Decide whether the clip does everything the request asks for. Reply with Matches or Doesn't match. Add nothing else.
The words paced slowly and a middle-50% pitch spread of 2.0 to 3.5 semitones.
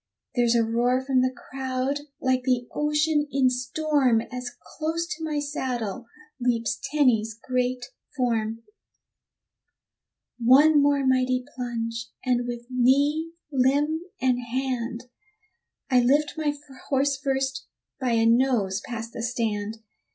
Matches